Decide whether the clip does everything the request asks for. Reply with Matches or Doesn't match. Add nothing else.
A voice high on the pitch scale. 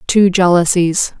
Doesn't match